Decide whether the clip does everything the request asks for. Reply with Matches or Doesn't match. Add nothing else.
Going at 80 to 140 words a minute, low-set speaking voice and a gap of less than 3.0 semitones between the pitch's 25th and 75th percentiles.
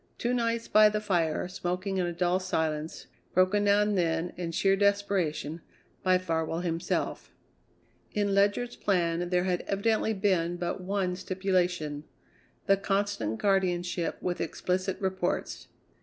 Doesn't match